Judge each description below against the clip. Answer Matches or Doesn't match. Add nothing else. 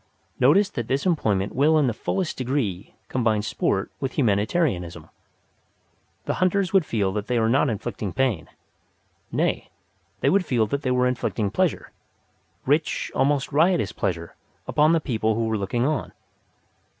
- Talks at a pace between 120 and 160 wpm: Matches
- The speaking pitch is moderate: Doesn't match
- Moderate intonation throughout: Doesn't match